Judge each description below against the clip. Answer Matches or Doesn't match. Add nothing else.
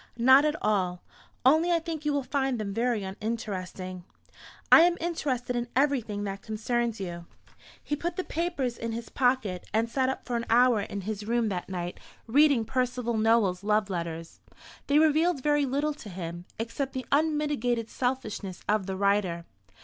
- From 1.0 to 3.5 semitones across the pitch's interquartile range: Doesn't match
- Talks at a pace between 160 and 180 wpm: Matches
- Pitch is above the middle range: Matches